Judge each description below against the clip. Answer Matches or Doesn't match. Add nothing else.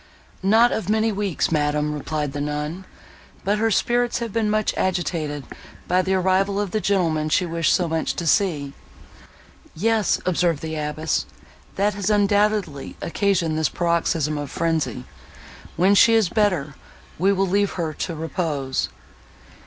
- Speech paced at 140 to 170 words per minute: Matches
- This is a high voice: Doesn't match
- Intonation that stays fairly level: Doesn't match